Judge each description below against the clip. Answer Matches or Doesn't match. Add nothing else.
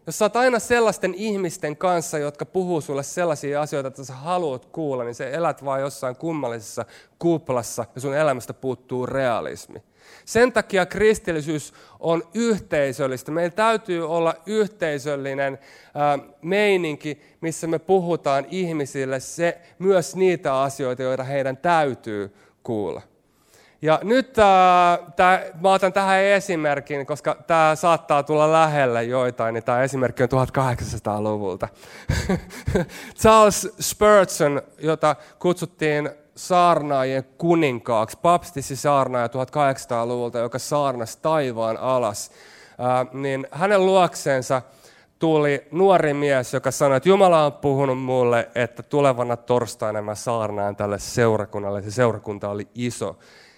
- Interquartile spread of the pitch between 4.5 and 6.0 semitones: Matches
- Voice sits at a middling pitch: Matches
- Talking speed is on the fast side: Doesn't match